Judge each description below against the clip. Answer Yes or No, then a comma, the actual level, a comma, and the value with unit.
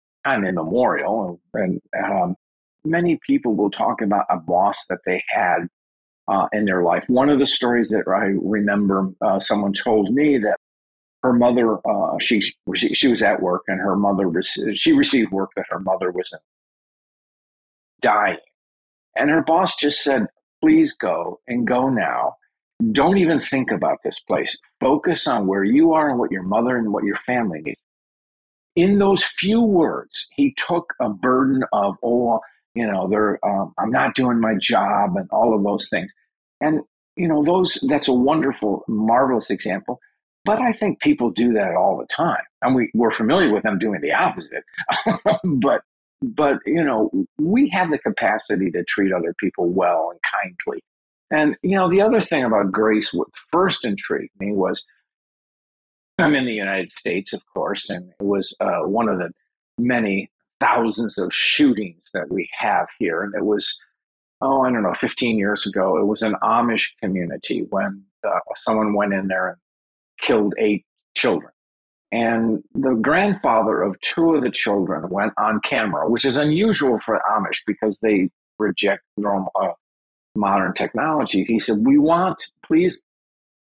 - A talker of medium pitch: No, low, 115 Hz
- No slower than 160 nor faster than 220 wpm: Yes, average, 170 wpm